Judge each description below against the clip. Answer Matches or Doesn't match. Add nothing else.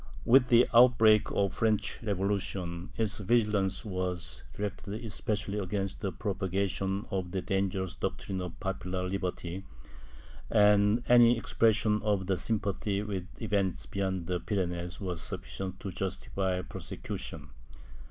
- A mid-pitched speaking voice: Doesn't match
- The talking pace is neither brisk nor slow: Doesn't match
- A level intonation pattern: Matches